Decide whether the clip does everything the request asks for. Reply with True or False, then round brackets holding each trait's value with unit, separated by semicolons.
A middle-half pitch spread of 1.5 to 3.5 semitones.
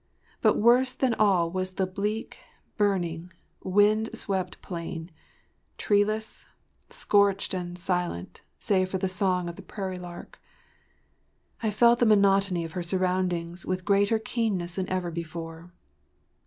True (2.7 semitones)